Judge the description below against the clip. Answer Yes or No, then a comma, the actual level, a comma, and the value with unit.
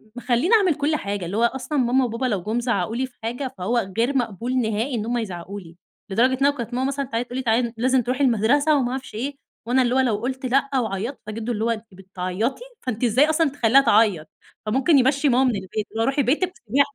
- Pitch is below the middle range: No, high, 245 Hz